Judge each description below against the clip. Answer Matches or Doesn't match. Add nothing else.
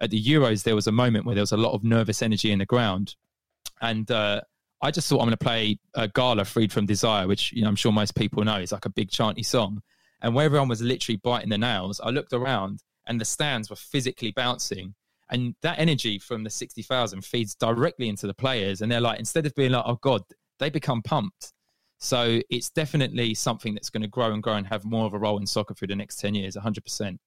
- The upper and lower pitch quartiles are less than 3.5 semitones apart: Matches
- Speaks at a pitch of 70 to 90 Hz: Doesn't match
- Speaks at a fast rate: Matches